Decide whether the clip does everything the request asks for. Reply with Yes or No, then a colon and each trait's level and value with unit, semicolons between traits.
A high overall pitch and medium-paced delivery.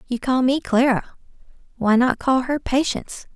Yes: very high, 255 Hz; average, 160 wpm